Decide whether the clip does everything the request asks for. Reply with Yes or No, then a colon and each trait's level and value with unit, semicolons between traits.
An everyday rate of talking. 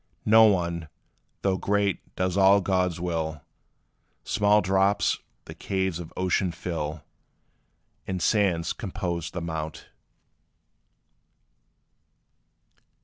No: slow, 90 wpm